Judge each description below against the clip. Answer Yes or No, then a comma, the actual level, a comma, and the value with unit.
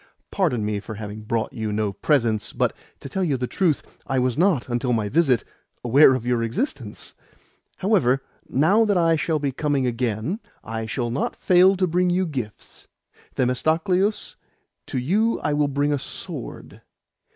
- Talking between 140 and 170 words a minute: Yes, average, 165 wpm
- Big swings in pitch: Yes, wide, 6.8 semitones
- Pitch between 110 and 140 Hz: Yes, low, 135 Hz